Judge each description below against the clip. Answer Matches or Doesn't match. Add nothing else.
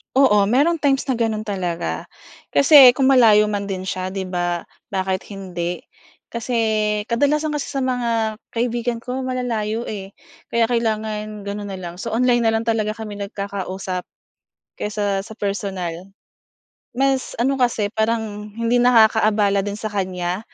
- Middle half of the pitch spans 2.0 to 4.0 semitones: Matches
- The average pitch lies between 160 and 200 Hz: Doesn't match